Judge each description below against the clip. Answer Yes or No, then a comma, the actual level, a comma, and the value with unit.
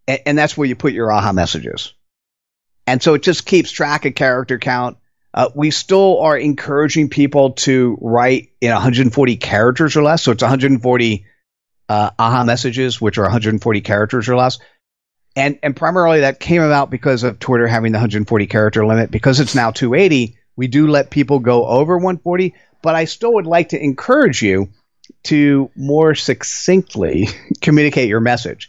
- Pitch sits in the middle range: No, low, 130 Hz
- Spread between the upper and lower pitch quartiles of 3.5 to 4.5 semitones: Yes, average, 4.1 semitones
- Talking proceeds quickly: No, average, 170 wpm